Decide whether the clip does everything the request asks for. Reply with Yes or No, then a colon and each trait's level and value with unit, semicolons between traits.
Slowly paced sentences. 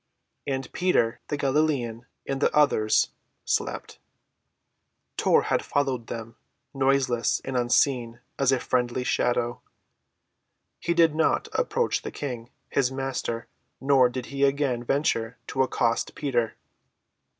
Yes: slow, 115 wpm